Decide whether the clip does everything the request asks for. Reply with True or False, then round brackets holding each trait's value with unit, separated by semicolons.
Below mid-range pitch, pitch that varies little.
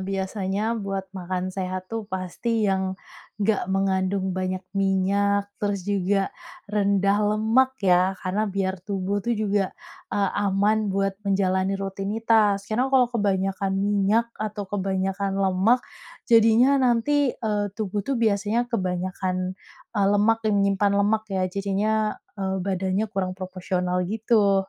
False (200 Hz; 2.1 semitones)